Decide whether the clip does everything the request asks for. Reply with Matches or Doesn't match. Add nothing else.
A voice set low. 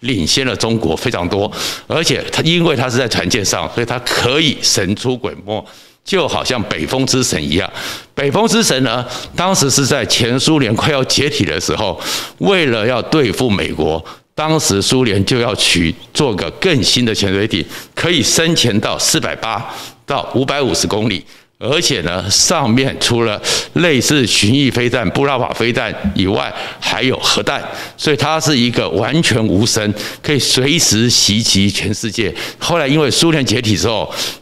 Matches